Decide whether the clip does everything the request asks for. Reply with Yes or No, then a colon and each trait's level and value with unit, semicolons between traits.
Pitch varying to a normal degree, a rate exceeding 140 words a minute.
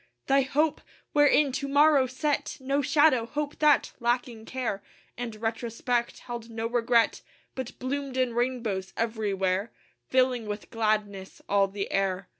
No: average, 3.8 semitones; slow, 135 wpm